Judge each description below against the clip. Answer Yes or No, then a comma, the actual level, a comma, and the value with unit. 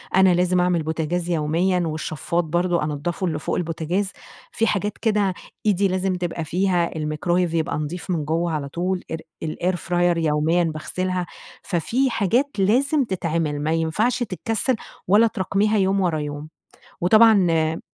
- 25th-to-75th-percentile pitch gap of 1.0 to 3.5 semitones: Yes, average, 3.2 semitones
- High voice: No, medium, 175 Hz